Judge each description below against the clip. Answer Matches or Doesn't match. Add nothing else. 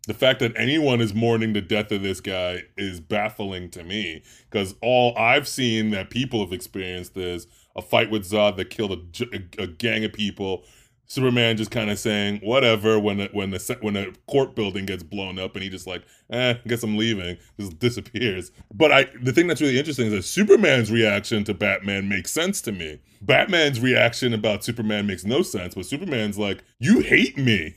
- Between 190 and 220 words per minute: Matches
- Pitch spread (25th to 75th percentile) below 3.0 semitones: Doesn't match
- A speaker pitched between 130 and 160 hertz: Doesn't match